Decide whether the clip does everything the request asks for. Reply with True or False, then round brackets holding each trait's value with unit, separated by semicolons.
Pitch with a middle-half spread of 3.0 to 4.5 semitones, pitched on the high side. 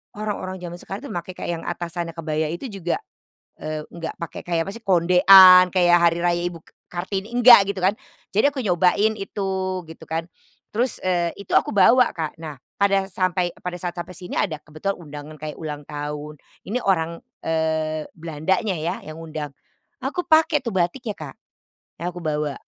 False (3.4 semitones; 175 Hz)